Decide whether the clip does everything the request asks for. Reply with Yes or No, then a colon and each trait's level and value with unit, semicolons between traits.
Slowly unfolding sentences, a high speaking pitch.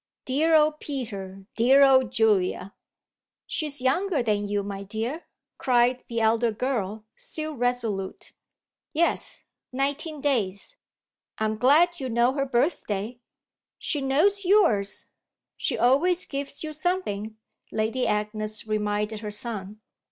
Yes: slow, 120 wpm; high, 245 Hz